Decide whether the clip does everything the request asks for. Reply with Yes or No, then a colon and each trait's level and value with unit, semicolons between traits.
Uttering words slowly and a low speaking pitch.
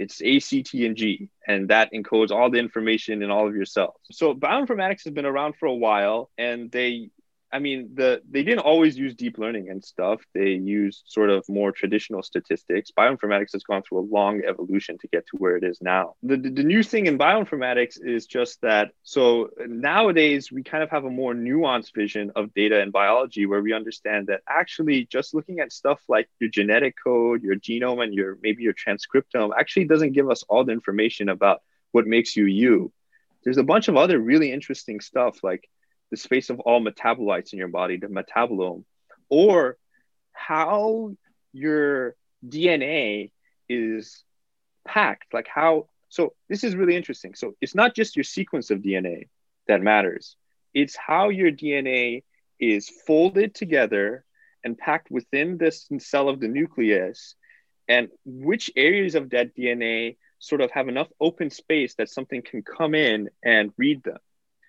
No: average, 180 wpm; low, 125 Hz